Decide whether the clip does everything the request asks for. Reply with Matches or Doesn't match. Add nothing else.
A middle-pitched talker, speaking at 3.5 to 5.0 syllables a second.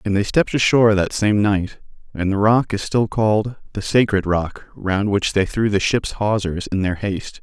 Doesn't match